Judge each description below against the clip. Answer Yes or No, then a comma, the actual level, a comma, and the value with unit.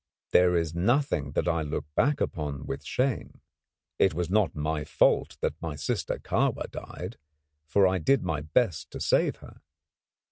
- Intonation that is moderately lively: Yes, average, 4.2 semitones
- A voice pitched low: Yes, very low, 85 Hz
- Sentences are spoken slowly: No, average, 165 wpm